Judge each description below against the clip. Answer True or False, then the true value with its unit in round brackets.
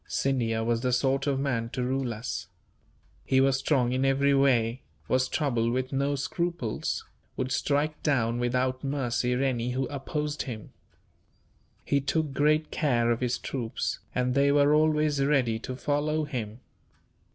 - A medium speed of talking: True (150 wpm)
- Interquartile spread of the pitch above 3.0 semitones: False (2.7 semitones)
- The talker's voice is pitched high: False (135 Hz)